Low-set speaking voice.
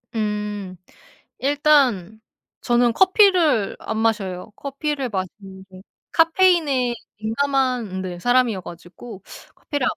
No: high, 235 Hz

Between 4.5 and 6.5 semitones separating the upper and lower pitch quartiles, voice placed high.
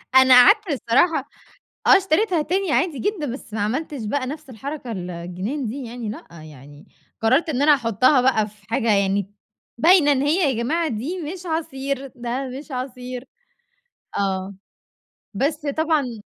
Yes: wide, 5.6 semitones; very high, 260 Hz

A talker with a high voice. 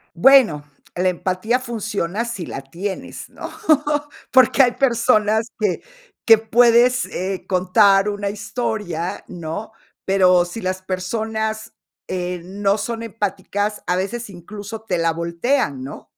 Yes: high, 205 Hz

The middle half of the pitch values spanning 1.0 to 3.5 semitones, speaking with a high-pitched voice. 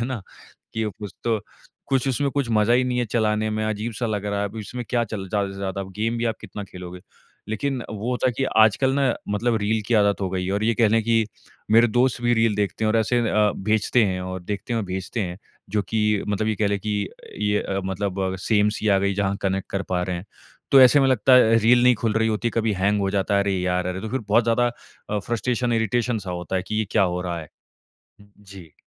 No: average, 3.0 semitones; low, 105 Hz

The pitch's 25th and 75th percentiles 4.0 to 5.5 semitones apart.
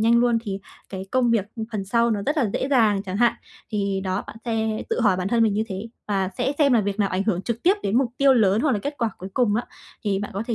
No: average, 3.3 semitones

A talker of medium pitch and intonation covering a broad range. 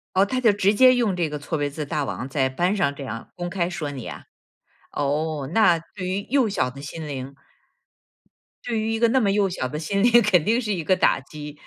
Yes: medium, 175 Hz; wide, 6.2 semitones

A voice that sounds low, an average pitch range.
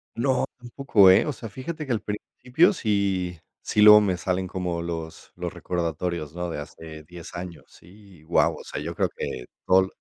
Yes: very low, 90 Hz; average, 3.8 semitones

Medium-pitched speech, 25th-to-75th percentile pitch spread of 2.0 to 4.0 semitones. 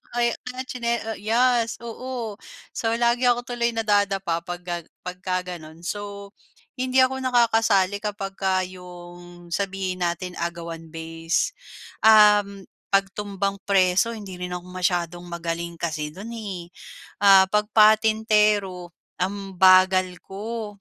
No: high, 195 Hz; average, 3.5 semitones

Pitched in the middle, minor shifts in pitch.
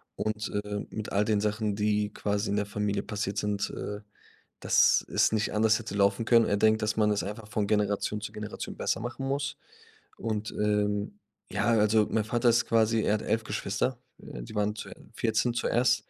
No: low, 105 Hz; narrow, 1.3 semitones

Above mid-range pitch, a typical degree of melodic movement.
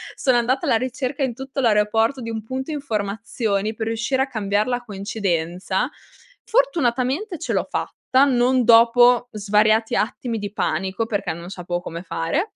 Yes: high, 230 Hz; average, 4.0 semitones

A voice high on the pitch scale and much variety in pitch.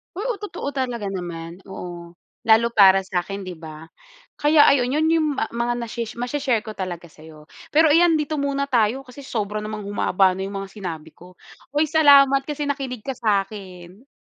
Yes: high, 220 Hz; wide, 6.7 semitones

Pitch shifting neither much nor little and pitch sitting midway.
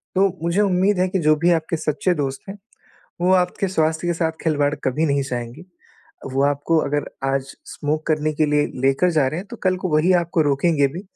Yes: average, 3.7 semitones; medium, 155 Hz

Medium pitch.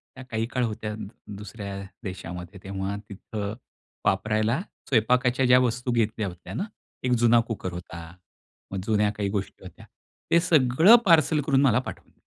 No: low, 110 Hz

